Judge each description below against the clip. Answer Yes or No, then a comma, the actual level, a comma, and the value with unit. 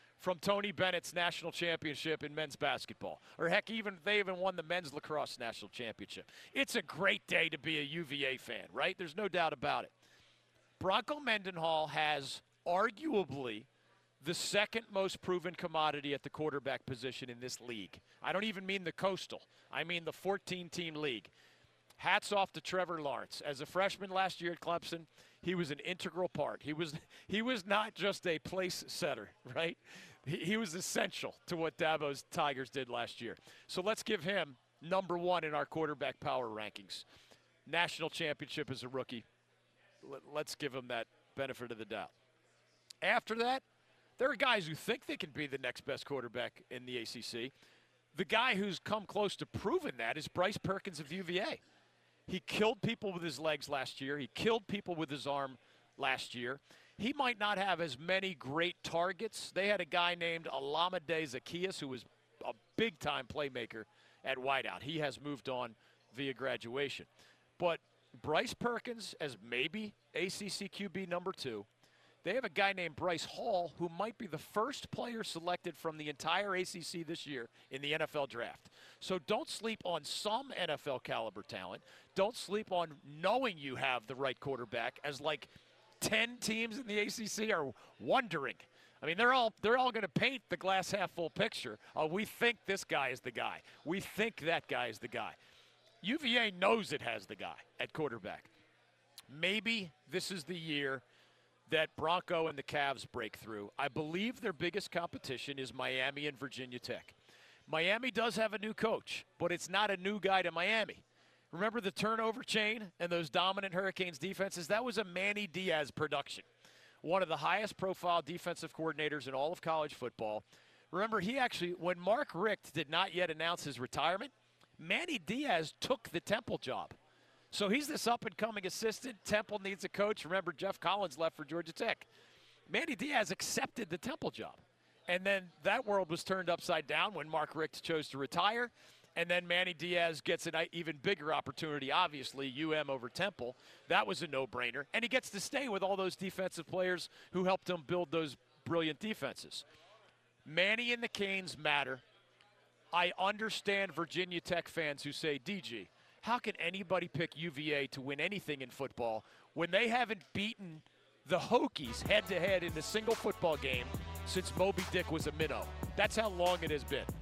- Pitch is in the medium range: Yes, medium, 175 Hz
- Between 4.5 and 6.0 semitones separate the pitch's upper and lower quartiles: Yes, average, 5.2 semitones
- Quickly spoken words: No, average, 180 wpm